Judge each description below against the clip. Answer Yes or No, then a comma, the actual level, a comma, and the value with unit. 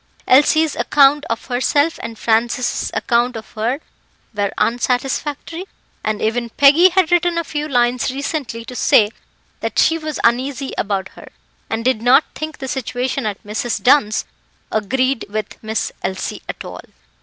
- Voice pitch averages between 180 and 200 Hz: No, very high, 250 Hz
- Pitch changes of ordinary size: Yes, average, 4.4 semitones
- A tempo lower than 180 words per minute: Yes, average, 150 wpm